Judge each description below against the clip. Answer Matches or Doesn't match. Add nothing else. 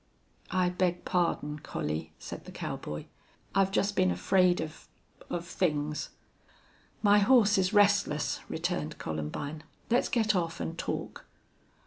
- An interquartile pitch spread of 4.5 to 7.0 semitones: Matches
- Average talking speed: Doesn't match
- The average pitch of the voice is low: Doesn't match